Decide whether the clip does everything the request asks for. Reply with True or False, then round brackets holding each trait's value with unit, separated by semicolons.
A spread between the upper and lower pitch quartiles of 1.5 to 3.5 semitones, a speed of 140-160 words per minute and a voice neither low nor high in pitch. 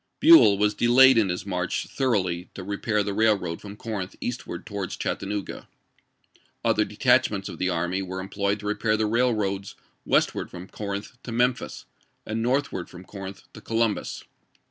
False (3.0 semitones; 155 wpm; 105 Hz)